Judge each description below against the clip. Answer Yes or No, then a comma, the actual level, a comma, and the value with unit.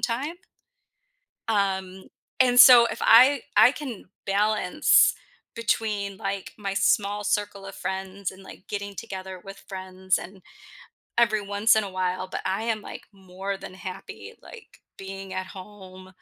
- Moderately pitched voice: No, high, 200 Hz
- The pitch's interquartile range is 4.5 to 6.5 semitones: No, narrow, 2.4 semitones